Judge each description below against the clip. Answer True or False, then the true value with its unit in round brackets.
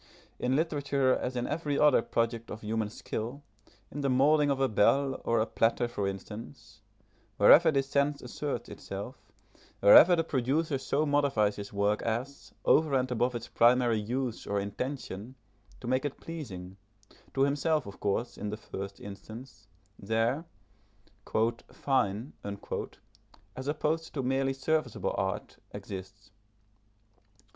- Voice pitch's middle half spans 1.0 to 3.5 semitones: False (4.7 semitones)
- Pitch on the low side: True (125 Hz)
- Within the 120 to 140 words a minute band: True (135 wpm)